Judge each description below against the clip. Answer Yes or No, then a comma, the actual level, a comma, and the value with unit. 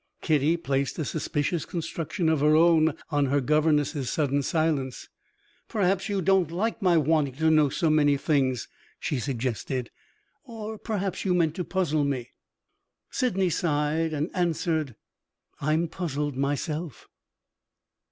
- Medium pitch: Yes, medium, 155 Hz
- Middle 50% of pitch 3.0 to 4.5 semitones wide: Yes, average, 3.3 semitones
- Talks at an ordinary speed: No, slow, 130 wpm